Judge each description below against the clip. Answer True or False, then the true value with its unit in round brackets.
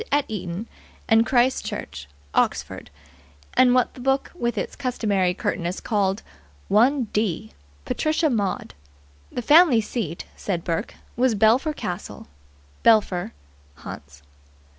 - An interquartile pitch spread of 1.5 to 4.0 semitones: False (5.5 semitones)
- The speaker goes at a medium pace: False (115 wpm)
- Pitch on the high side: True (220 Hz)